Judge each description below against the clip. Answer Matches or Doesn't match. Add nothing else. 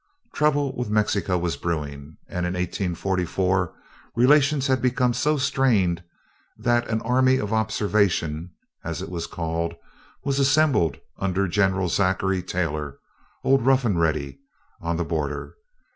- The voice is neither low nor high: Doesn't match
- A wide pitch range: Matches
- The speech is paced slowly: Matches